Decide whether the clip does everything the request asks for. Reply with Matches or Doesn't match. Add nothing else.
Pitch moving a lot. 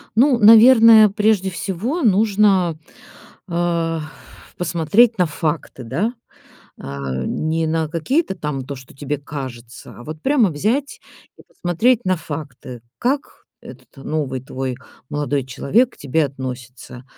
Matches